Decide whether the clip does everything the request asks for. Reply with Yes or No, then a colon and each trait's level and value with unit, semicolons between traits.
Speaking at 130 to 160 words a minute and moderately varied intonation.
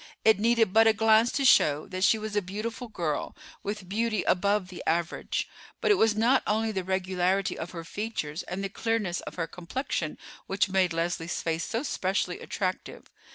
No: average, 185 wpm; average, 3.8 semitones